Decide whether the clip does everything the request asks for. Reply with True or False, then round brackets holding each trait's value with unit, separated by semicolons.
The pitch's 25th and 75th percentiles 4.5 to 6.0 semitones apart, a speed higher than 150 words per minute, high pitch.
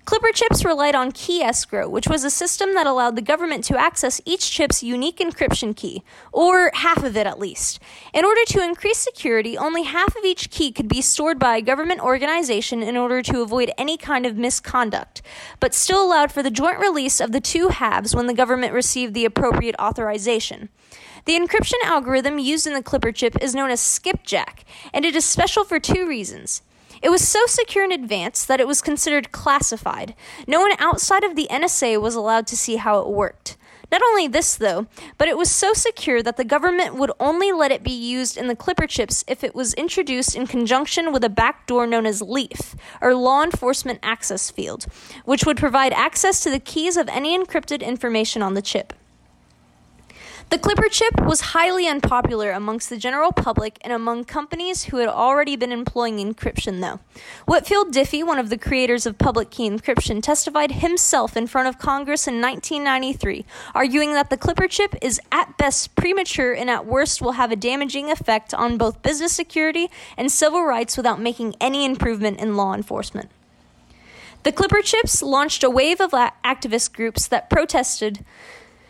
True (5.6 semitones; 185 wpm; 270 Hz)